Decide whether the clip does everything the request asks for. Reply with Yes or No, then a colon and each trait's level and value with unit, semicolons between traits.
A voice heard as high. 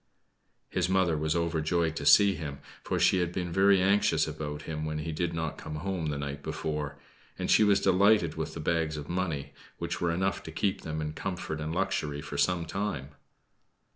No: very low, 80 Hz